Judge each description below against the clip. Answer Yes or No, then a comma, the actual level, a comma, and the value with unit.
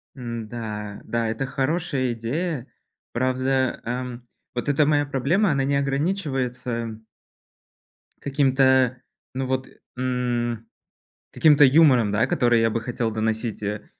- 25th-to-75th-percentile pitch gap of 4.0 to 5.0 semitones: No, average, 2.8 semitones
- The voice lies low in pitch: Yes, low, 125 Hz